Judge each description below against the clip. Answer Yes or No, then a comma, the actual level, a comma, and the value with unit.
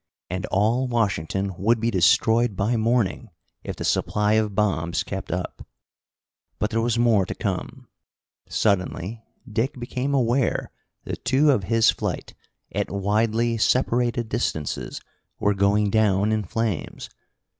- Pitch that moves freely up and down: No, average, 3.0 semitones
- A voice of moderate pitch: No, low, 110 Hz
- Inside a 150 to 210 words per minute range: No, slow, 135 wpm